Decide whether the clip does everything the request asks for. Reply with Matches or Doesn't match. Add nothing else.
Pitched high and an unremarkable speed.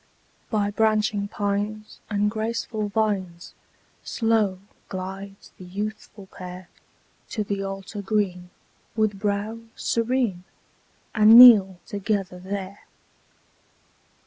Doesn't match